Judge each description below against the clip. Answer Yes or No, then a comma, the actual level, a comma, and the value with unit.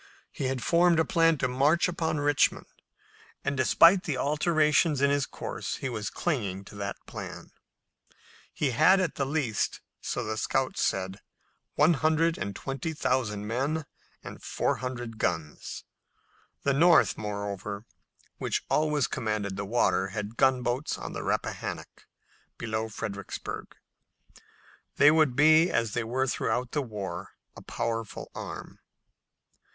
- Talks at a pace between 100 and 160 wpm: Yes, average, 140 wpm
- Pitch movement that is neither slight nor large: No, wide, 6.0 semitones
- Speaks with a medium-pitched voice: No, low, 130 Hz